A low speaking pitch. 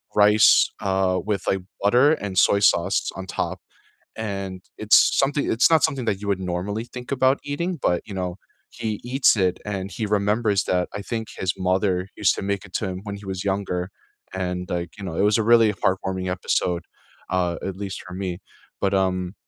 Yes: low, 100 Hz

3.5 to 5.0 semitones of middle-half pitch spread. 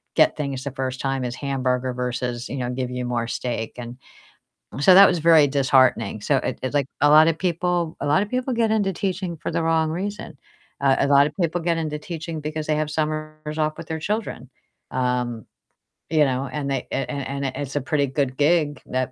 Yes: average, 3.9 semitones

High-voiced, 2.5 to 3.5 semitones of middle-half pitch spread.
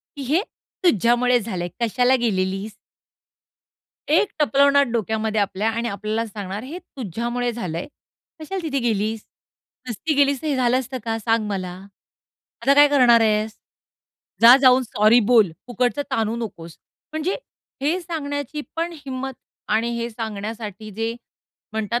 No: high, 235 Hz; average, 4.1 semitones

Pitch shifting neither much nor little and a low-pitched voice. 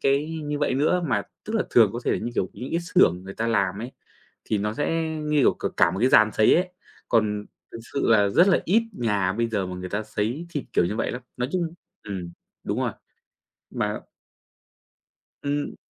No: wide, 6.3 semitones; low, 115 Hz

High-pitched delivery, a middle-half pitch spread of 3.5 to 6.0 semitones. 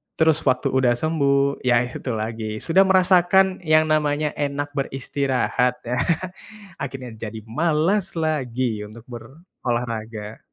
No: low, 135 Hz; average, 4.9 semitones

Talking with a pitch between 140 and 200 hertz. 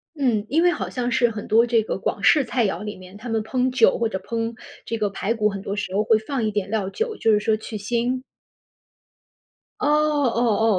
No: high, 225 Hz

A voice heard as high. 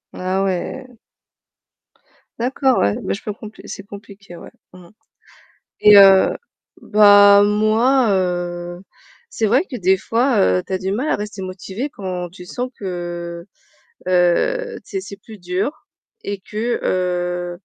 Yes: high, 200 Hz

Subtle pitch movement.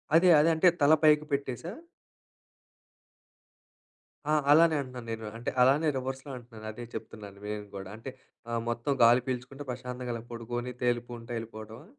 No: average, 3.2 semitones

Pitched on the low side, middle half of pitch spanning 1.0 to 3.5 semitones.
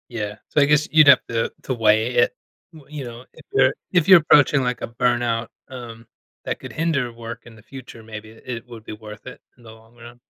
Yes: low, 120 Hz; average, 2.9 semitones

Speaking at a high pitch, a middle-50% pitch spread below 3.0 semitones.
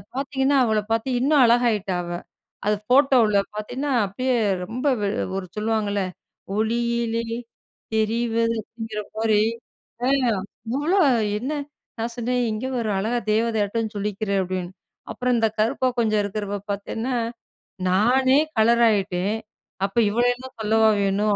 Yes: high, 225 Hz; narrow, 2.6 semitones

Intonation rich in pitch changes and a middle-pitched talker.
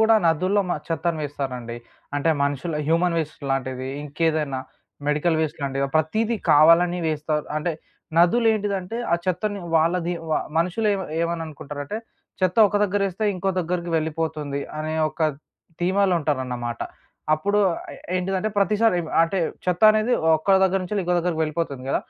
No: average, 4.0 semitones; medium, 165 Hz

